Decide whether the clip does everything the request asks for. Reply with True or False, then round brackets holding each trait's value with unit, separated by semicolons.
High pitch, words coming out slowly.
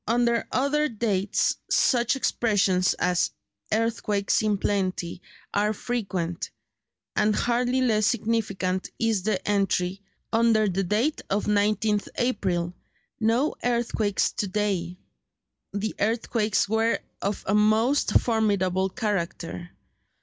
True (210 Hz; 105 wpm)